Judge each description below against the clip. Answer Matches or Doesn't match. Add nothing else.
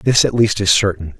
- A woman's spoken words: Doesn't match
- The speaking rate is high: Matches